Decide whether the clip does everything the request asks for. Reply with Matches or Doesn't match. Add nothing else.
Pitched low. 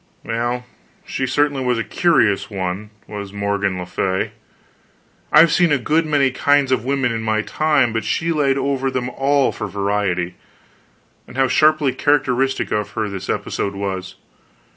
Matches